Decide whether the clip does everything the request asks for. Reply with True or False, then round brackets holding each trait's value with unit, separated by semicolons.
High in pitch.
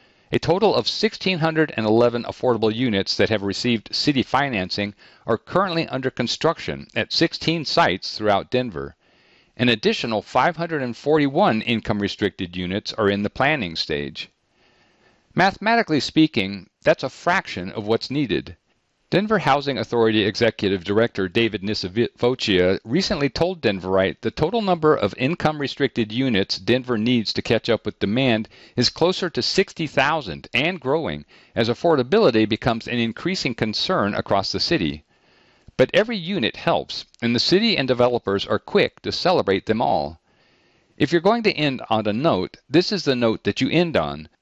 False (120 Hz)